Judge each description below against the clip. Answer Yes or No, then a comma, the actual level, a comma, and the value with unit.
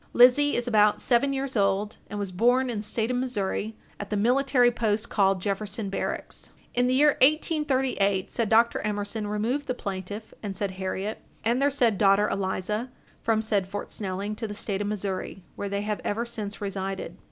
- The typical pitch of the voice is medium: No, high, 210 Hz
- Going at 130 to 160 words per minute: No, average, 185 wpm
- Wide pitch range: No, average, 3.4 semitones